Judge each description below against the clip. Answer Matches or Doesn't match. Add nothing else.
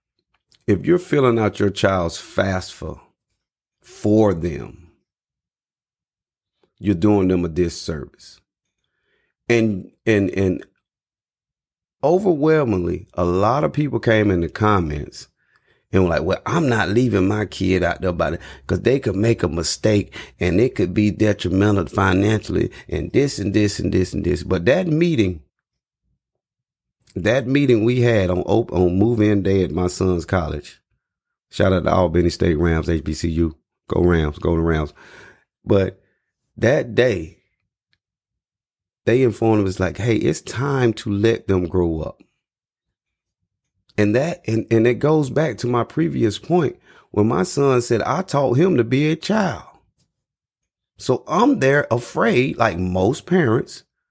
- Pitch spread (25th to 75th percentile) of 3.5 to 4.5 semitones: Doesn't match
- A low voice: Matches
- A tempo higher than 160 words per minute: Doesn't match